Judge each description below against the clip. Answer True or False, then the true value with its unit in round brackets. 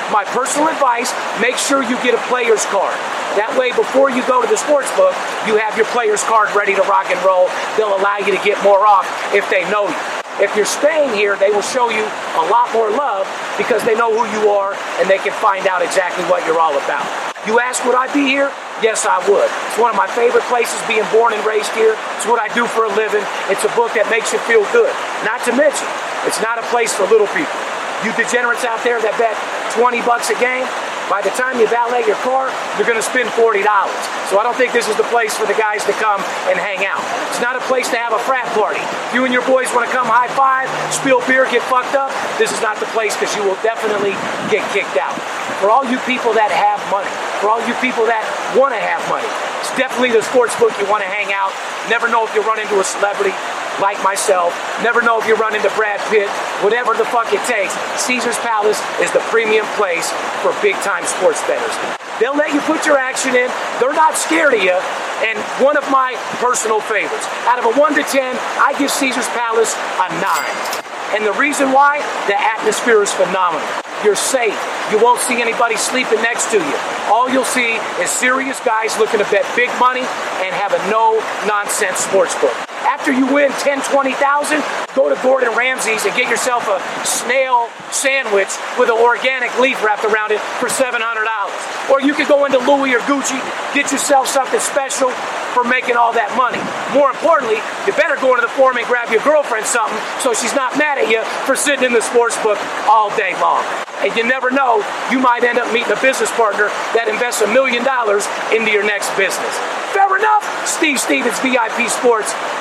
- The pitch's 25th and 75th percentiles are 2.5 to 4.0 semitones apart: True (3.7 semitones)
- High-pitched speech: True (245 Hz)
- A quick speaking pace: True (215 wpm)